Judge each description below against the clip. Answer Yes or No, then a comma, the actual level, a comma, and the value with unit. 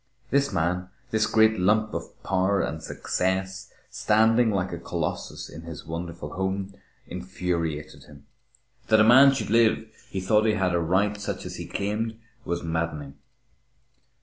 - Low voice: Yes, very low, 95 Hz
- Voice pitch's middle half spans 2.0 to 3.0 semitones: No, average, 4.3 semitones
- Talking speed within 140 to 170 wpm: Yes, average, 150 wpm